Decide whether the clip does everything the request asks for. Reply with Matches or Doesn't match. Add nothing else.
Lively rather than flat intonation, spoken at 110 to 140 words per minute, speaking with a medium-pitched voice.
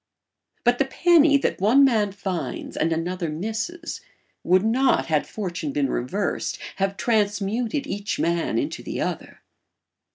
Doesn't match